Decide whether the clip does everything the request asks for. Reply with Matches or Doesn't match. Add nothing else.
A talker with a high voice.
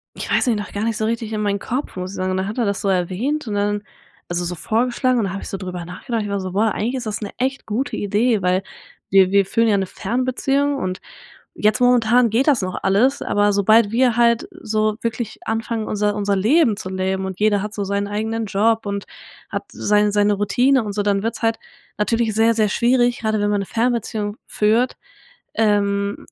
Matches